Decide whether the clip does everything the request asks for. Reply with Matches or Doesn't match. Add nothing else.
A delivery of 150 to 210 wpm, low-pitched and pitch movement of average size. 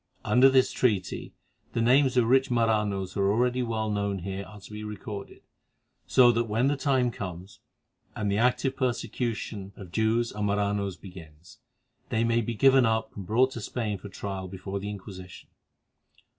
Matches